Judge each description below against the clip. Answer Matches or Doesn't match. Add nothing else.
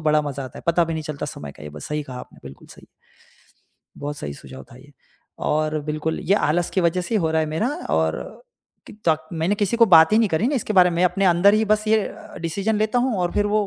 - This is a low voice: Doesn't match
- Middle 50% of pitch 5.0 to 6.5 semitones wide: Matches